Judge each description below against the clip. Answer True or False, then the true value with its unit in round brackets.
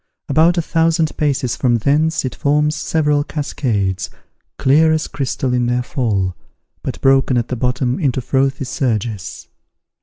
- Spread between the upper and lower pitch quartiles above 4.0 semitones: False (3.6 semitones)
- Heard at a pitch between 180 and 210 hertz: False (135 Hz)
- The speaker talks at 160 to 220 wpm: False (145 wpm)